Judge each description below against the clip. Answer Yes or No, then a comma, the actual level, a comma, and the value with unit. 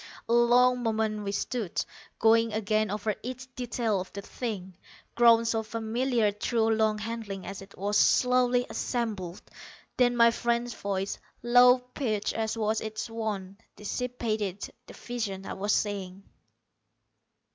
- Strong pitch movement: No, narrow, 2.6 semitones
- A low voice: No, high, 220 Hz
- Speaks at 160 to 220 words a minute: No, slow, 135 wpm